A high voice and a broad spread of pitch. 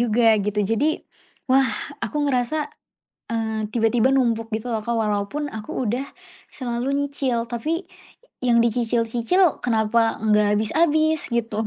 No: high, 235 Hz; average, 3.5 semitones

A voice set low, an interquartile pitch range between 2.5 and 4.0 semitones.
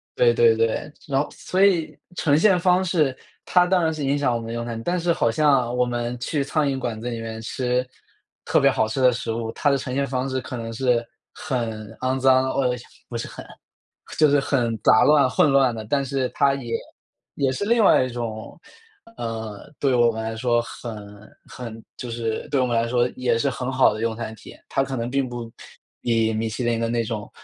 Yes: low, 125 Hz; average, 3.1 semitones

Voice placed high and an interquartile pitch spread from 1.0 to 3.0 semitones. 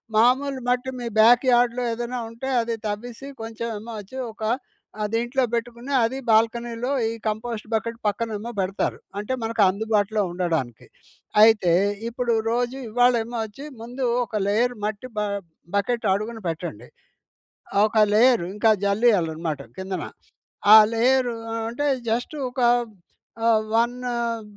Yes: high, 230 Hz; narrow, 2.5 semitones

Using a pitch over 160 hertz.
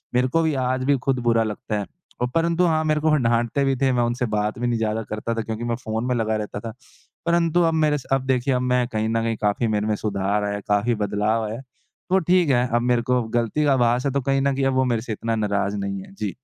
No: low, 120 Hz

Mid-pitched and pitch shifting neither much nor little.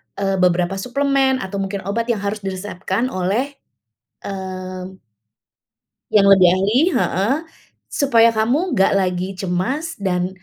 No: high, 195 Hz; average, 3.9 semitones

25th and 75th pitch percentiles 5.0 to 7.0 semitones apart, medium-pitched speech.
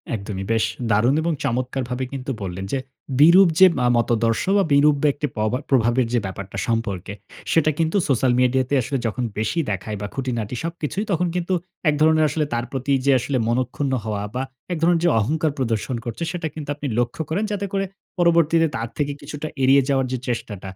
No: average, 5.3 semitones; low, 130 Hz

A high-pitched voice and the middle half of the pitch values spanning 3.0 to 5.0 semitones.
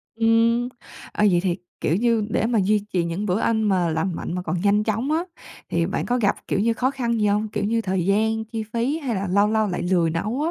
Yes: high, 210 Hz; average, 3.4 semitones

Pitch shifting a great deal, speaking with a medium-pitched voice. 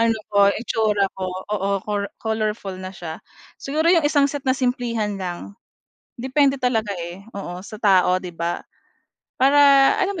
No: wide, 5.9 semitones; high, 215 Hz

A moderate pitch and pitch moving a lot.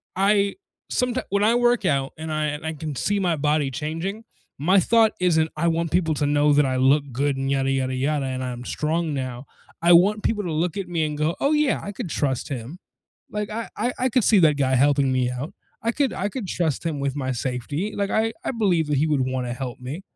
Yes: medium, 155 Hz; wide, 6.4 semitones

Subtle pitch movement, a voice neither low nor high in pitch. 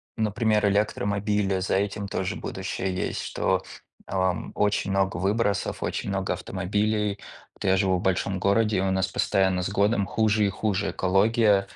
No: narrow, 1.6 semitones; low, 100 Hz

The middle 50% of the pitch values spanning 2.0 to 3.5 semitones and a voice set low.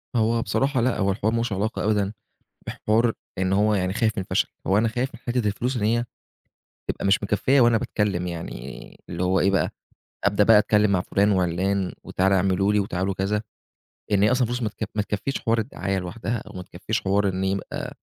Yes: average, 2.7 semitones; low, 105 Hz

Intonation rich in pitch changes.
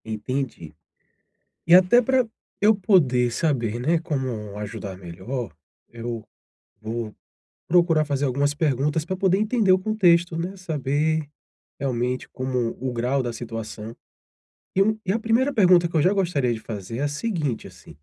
Yes: wide, 7.3 semitones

